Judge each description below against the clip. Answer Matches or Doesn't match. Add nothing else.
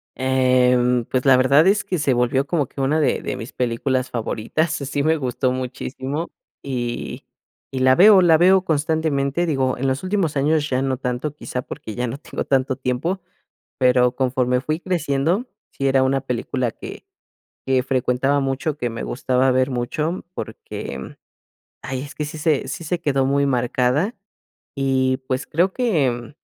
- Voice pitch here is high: Doesn't match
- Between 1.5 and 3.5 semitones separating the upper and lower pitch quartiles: Matches